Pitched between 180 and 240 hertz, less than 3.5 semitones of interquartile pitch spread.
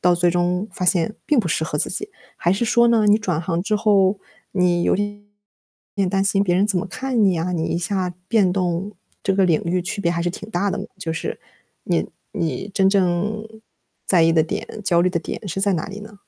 Yes: high, 190 Hz; average, 2.9 semitones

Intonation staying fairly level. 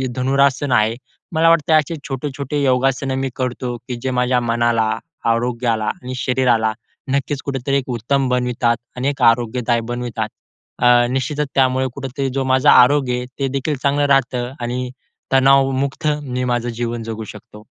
Yes: narrow, 2.2 semitones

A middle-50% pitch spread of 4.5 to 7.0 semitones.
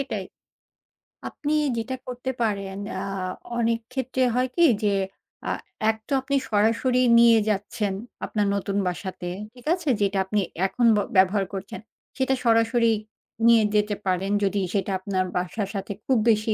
No: average, 3.8 semitones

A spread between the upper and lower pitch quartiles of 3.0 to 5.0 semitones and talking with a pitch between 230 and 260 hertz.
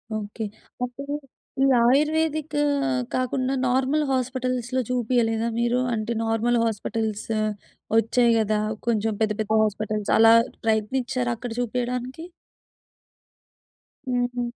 No: narrow, 2.5 semitones; high, 240 Hz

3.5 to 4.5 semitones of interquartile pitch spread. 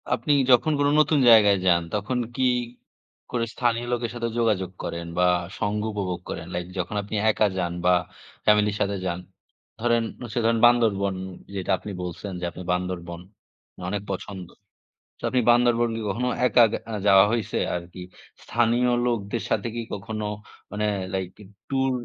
Yes: average, 4.1 semitones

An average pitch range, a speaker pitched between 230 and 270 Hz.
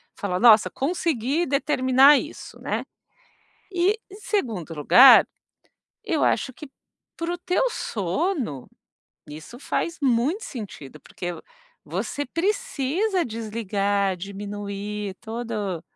No: wide, 8.0 semitones; high, 235 Hz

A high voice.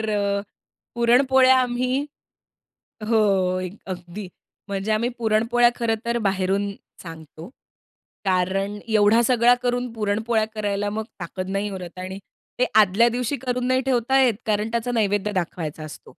Yes: high, 215 Hz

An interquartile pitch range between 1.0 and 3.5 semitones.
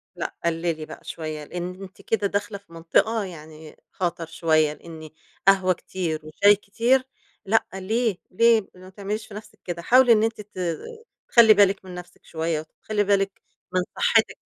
No: average, 4.1 semitones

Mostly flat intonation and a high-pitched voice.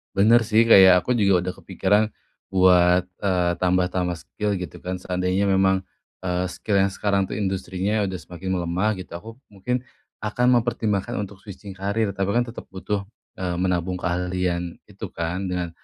No: narrow, 2.2 semitones; very low, 95 Hz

